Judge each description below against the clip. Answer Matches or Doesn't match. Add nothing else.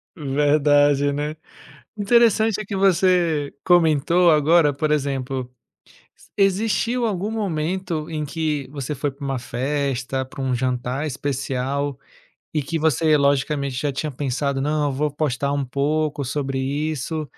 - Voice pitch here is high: Doesn't match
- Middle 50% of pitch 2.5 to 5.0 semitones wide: Matches